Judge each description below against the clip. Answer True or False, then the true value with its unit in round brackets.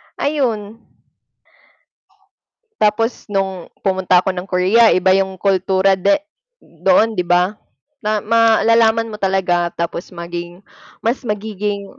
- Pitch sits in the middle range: False (195 Hz)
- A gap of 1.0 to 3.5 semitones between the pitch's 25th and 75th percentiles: True (3.2 semitones)